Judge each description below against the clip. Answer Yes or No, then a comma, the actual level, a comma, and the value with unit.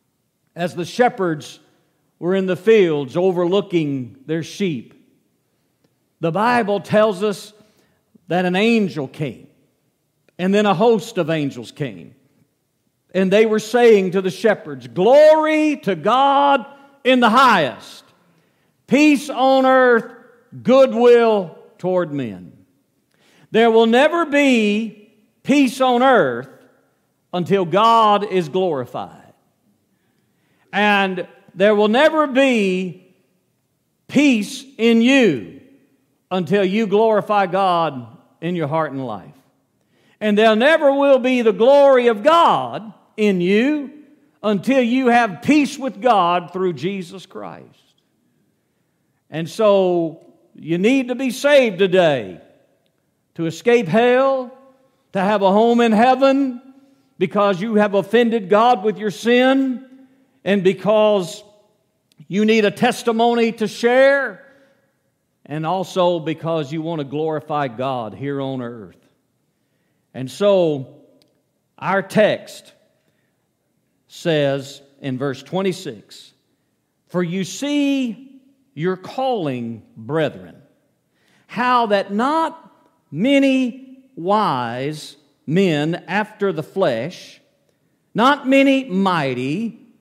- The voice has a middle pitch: No, high, 205 Hz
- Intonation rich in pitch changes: Yes, wide, 6.7 semitones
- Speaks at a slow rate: Yes, slow, 110 wpm